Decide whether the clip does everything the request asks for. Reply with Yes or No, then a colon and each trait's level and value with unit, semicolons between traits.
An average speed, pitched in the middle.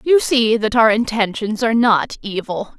No: average, 170 wpm; high, 220 Hz